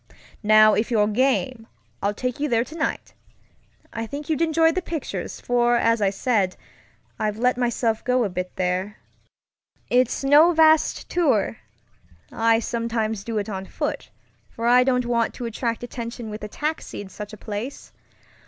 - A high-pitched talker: Yes, high, 230 Hz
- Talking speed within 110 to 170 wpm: Yes, average, 160 wpm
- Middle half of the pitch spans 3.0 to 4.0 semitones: Yes, average, 3.3 semitones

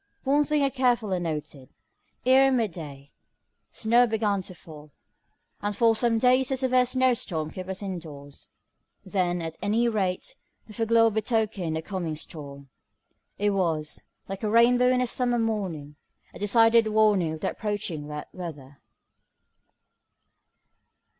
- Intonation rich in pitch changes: Yes, wide, 6.4 semitones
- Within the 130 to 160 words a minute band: Yes, average, 140 wpm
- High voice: Yes, high, 205 Hz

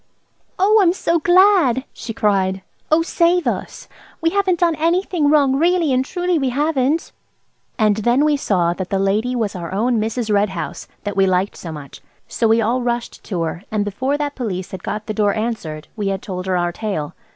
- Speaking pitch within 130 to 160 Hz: No, high, 230 Hz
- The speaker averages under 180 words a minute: No, fast, 205 wpm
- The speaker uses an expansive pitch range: Yes, wide, 7.7 semitones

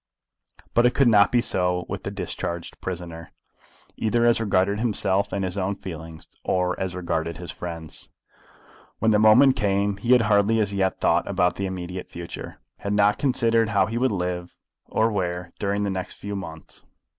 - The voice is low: Yes, low, 100 Hz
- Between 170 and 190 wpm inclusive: Yes, average, 180 wpm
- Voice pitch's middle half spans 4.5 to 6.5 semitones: No, average, 3.3 semitones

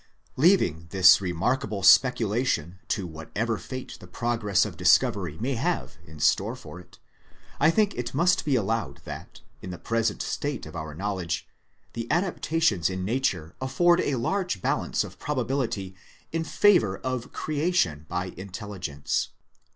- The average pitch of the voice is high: No, low, 110 Hz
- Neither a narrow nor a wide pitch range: No, wide, 7.0 semitones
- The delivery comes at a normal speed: Yes, average, 145 wpm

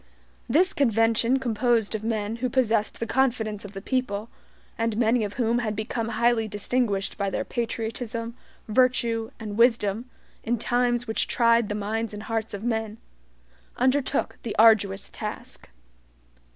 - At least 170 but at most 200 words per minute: No, average, 145 wpm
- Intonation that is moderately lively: No, narrow, 2.1 semitones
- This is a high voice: Yes, high, 225 Hz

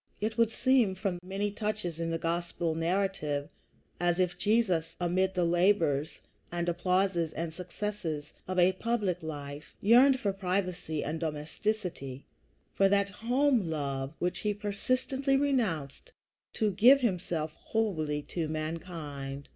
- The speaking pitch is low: No, medium, 180 Hz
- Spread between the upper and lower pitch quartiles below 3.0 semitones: No, average, 4.5 semitones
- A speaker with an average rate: No, slow, 130 wpm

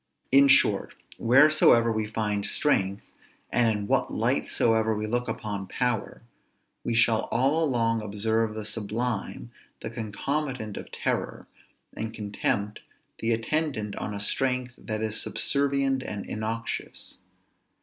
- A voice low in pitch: Yes, low, 115 Hz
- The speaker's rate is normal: No, slow, 130 wpm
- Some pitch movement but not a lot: Yes, average, 3.0 semitones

